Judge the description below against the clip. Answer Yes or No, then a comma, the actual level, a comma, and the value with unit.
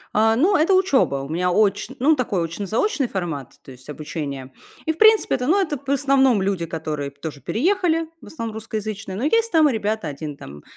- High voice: Yes, high, 220 Hz